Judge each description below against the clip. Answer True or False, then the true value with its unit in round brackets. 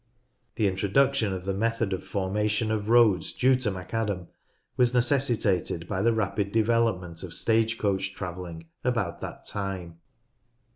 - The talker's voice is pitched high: False (105 Hz)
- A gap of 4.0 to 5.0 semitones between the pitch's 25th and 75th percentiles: False (3.5 semitones)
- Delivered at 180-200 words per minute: False (140 wpm)